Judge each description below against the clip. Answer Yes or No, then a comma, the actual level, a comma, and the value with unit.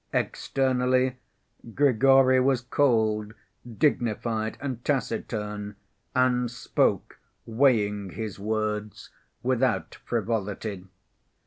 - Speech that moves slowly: Yes, slow, 75 wpm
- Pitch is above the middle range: No, low, 115 Hz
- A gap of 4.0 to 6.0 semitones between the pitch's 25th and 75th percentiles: No, average, 3.4 semitones